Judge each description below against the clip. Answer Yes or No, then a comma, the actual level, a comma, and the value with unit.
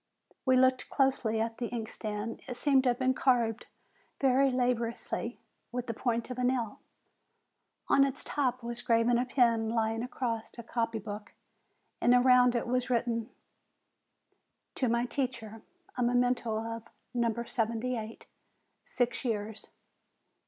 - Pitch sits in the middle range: No, high, 240 Hz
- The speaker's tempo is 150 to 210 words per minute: No, average, 140 wpm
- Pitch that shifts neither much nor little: No, narrow, 1.8 semitones